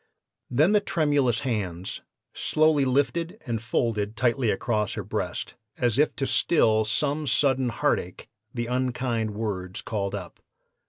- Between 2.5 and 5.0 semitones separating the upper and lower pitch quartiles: Yes, average, 4.6 semitones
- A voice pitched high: No, low, 120 Hz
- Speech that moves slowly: Yes, slow, 130 wpm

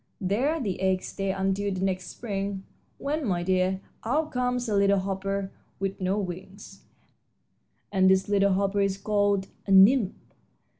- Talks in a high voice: Yes, high, 195 Hz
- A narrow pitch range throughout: Yes, narrow, 1.3 semitones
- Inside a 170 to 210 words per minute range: No, average, 145 wpm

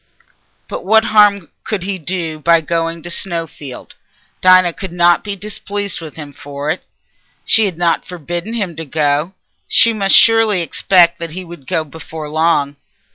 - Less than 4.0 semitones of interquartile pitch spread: Yes, average, 3.6 semitones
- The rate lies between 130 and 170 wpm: Yes, average, 165 wpm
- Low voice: No, medium, 170 Hz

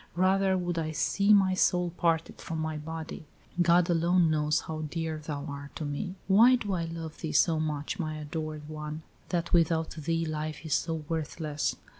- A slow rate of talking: No, average, 180 wpm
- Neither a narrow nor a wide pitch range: No, narrow, 2.2 semitones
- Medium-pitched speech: Yes, medium, 160 Hz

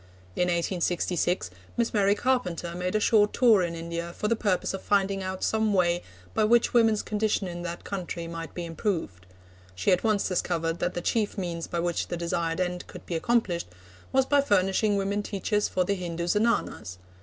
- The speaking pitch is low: No, medium, 185 Hz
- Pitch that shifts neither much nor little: Yes, average, 3.4 semitones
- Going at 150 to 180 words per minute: No, average, 190 wpm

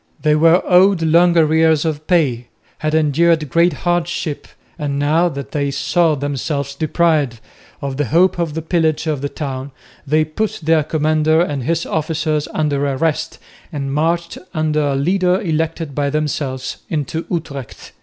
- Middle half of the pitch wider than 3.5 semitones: No, narrow, 2.5 semitones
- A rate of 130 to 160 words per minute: Yes, average, 155 wpm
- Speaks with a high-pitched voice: No, medium, 155 Hz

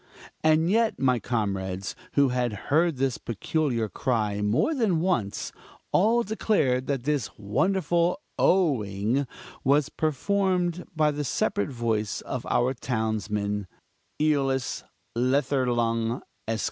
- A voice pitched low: Yes, low, 130 Hz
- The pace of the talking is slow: Yes, slow, 115 wpm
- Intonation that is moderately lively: No, wide, 6.1 semitones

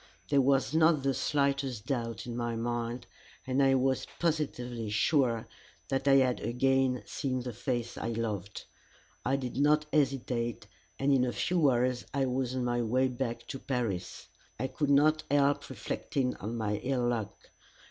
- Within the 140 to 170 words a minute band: Yes, average, 165 wpm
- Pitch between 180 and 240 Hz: No, low, 130 Hz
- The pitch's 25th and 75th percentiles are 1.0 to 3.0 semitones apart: Yes, narrow, 2.6 semitones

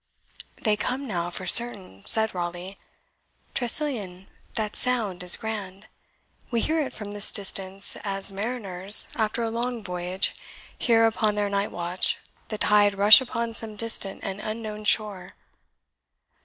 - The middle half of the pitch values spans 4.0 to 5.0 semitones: No, average, 2.9 semitones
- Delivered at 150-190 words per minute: No, average, 140 wpm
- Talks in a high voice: Yes, high, 210 Hz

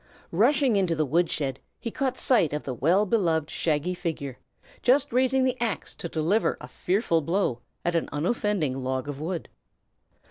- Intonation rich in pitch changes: Yes, wide, 7.0 semitones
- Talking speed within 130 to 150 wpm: No, average, 170 wpm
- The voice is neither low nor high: Yes, medium, 175 Hz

